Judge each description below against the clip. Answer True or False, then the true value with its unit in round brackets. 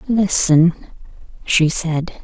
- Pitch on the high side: False (170 Hz)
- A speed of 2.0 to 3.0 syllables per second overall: True (2.9 syllables/s)